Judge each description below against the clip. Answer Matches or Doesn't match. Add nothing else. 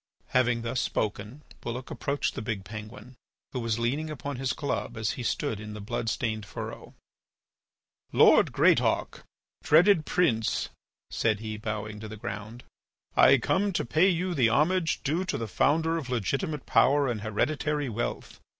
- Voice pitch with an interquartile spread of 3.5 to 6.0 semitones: Matches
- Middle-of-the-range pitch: Doesn't match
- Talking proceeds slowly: Doesn't match